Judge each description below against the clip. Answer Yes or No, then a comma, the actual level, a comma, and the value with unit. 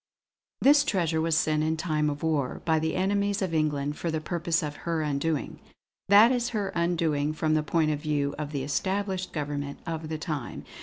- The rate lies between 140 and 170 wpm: No, average, 195 wpm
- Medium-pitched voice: Yes, medium, 160 Hz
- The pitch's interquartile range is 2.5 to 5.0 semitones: Yes, average, 2.9 semitones